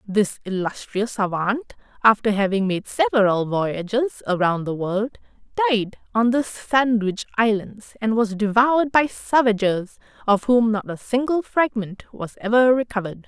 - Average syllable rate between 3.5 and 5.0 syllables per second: Yes, 4.5 syllables/s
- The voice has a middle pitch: No, high, 220 Hz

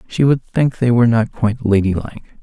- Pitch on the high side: No, low, 115 Hz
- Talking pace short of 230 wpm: Yes, average, 200 wpm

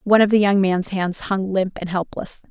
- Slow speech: No, fast, 240 wpm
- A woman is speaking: Yes, female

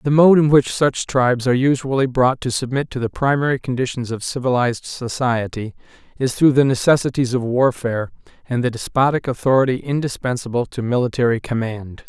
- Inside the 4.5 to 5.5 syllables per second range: No, 5.7 syllables/s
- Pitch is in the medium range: No, low, 125 Hz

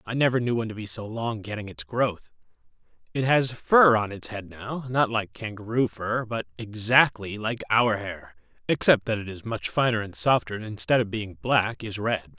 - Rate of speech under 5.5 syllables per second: Yes, 4.9 syllables/s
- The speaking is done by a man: Yes, male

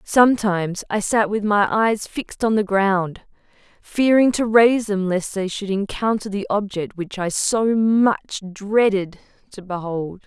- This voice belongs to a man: No, female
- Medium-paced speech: Yes, average, 160 wpm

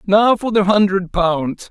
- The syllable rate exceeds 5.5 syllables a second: No, 3.7 syllables/s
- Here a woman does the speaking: No, male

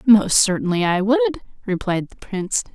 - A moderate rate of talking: Yes, average, 155 wpm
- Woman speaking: Yes, female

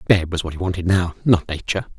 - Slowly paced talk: No, fast, 240 wpm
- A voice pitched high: No, very low, 90 Hz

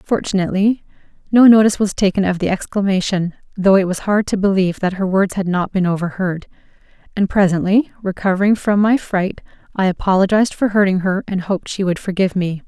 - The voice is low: No, high, 195 Hz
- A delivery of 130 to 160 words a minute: No, average, 180 wpm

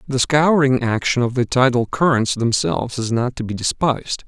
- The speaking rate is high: No, average, 185 wpm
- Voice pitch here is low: Yes, low, 125 Hz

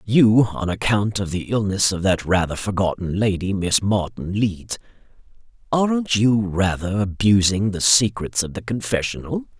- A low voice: Yes, low, 100 Hz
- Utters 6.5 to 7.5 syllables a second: No, 4.6 syllables/s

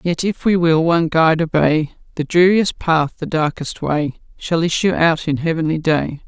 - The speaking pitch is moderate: Yes, medium, 165 Hz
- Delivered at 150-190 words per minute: Yes, average, 180 wpm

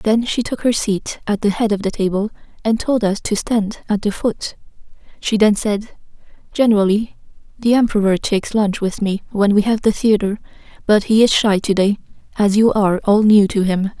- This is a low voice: No, high, 210 Hz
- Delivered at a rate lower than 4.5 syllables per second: No, 5.1 syllables/s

